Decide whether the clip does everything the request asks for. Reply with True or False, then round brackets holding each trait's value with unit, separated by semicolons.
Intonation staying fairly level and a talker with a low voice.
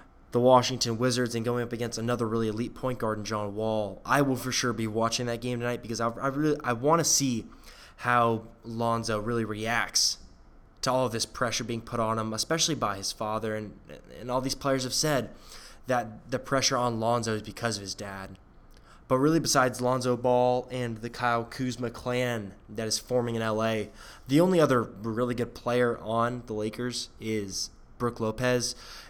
True (2.2 semitones; 120 Hz)